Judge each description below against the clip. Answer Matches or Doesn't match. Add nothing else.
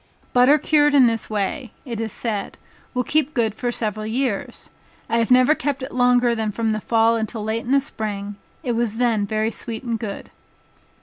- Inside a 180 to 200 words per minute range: Matches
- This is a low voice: Doesn't match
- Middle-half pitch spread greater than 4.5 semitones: Doesn't match